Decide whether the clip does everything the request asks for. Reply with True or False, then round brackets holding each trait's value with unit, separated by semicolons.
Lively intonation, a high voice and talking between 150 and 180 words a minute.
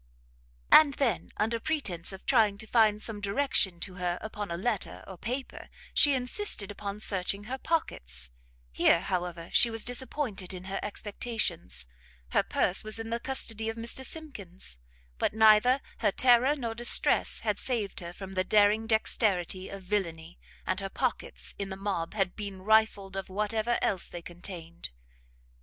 False (3.7 semitones; 205 Hz; 160 wpm)